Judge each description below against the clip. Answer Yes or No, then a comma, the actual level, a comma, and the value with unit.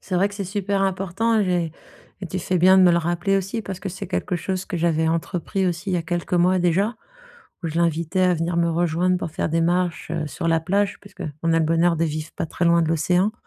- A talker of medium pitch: Yes, medium, 175 Hz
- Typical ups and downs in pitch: No, narrow, 2.3 semitones